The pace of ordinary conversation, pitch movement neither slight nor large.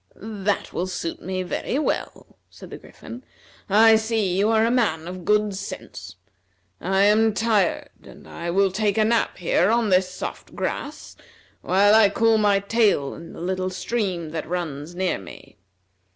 Yes: average, 165 wpm; average, 3.4 semitones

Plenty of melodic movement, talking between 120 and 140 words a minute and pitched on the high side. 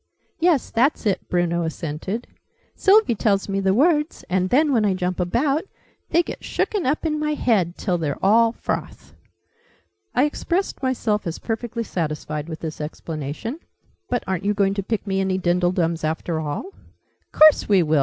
No: wide, 7.0 semitones; average, 165 wpm; high, 195 Hz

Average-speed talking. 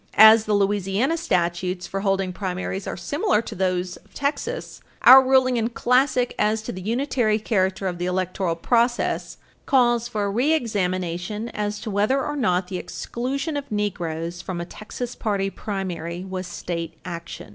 Yes: average, 160 wpm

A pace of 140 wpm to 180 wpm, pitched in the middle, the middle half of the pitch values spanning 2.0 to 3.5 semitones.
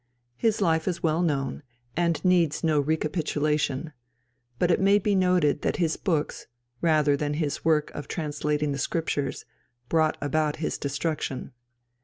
Yes: average, 145 wpm; medium, 155 Hz; narrow, 2.4 semitones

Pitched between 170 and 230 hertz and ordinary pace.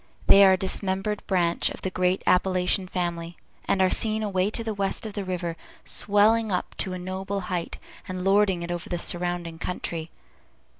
Yes: medium, 185 Hz; average, 185 wpm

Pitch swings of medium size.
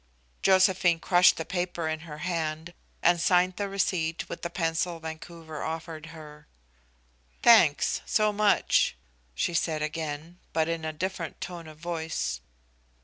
No: narrow, 2.0 semitones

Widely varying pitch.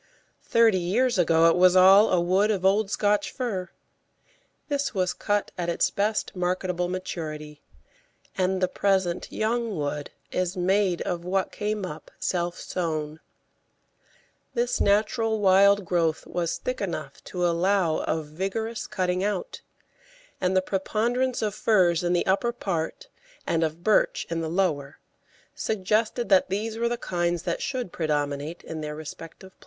No: average, 3.4 semitones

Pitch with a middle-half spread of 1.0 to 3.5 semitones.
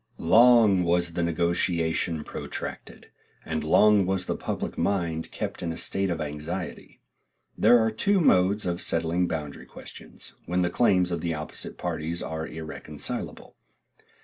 Yes: average, 2.9 semitones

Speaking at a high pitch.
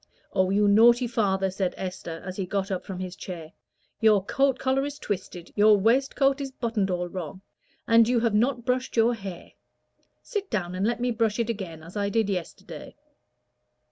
Yes: high, 210 Hz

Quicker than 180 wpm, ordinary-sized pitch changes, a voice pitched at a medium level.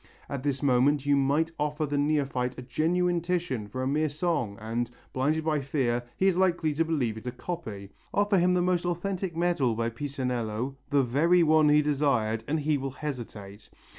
Yes: average, 190 wpm; average, 4.7 semitones; medium, 145 Hz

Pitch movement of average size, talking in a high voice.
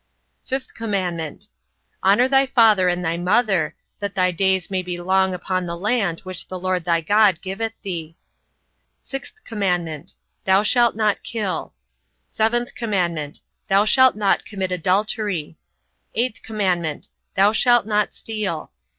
Yes: average, 3.6 semitones; high, 195 Hz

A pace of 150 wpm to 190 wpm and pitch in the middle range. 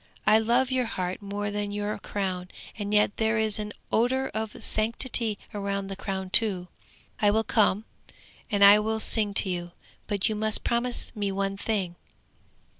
No: average, 170 wpm; high, 210 Hz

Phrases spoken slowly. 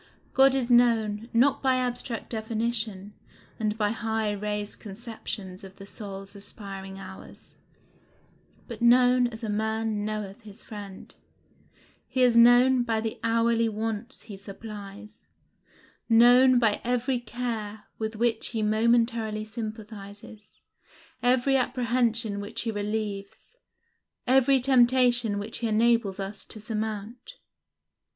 Yes: slow, 120 wpm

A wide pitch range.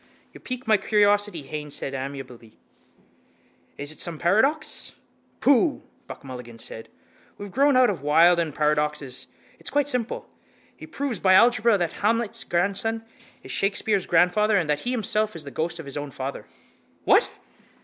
Yes: wide, 7.0 semitones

